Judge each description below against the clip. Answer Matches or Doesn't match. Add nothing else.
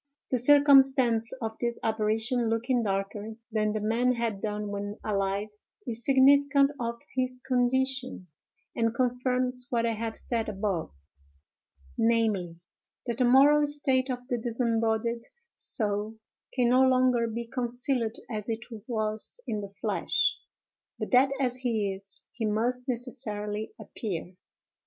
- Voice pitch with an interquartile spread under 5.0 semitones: Matches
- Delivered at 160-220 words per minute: Doesn't match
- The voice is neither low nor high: Doesn't match